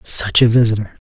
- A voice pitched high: No, low, 110 Hz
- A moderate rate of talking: Yes, average, 170 wpm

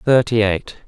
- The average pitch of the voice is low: Yes, low, 110 Hz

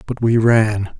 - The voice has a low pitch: Yes, low, 110 Hz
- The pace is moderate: Yes, average, 180 wpm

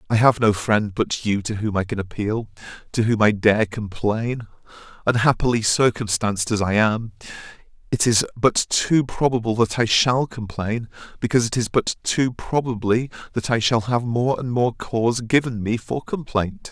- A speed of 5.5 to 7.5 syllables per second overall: No, 4.7 syllables/s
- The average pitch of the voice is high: No, low, 115 Hz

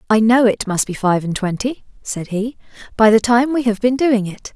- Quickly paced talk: Yes, fast, 235 wpm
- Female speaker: Yes, female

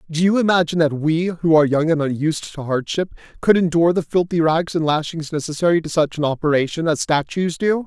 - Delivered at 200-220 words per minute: Yes, fast, 205 wpm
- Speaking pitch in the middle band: Yes, medium, 165 Hz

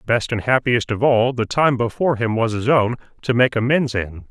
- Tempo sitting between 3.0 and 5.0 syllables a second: No, 5.2 syllables/s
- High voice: No, low, 120 Hz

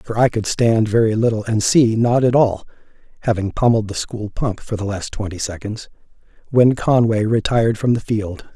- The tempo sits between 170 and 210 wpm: Yes, average, 190 wpm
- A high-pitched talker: No, low, 110 Hz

